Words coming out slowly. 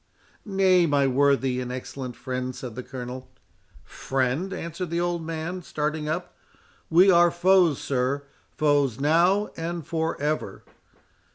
Yes: slow, 120 wpm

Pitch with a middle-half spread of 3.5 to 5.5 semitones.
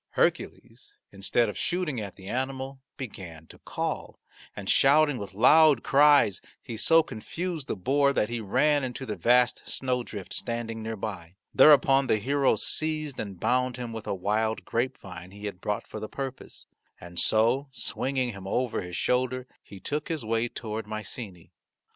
Yes: average, 4.6 semitones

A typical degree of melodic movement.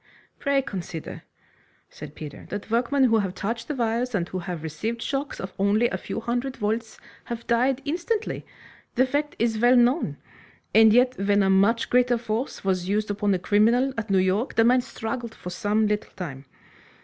Yes: average, 3.8 semitones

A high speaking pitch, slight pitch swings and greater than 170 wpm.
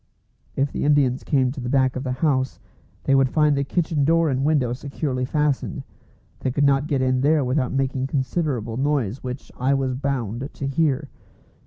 No: low, 135 Hz; narrow, 2.1 semitones; average, 185 wpm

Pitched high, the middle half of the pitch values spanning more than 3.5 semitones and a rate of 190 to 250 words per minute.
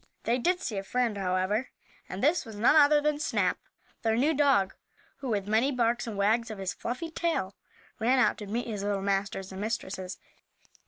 Yes: high, 225 Hz; average, 4.8 semitones; average, 195 wpm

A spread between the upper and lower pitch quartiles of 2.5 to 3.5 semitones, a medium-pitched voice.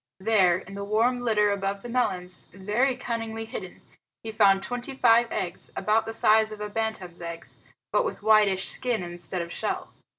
No: average, 3.1 semitones; high, 215 Hz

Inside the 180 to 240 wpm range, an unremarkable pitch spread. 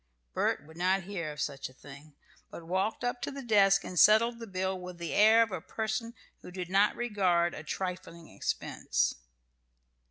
Yes: average, 185 wpm; average, 4.1 semitones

